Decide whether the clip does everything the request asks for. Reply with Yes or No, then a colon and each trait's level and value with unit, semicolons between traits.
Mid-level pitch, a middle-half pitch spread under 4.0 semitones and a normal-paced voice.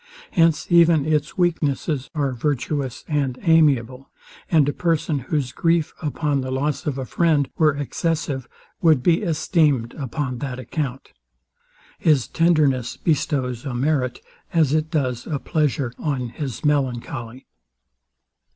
No: medium, 145 Hz; average, 3.3 semitones; slow, 130 wpm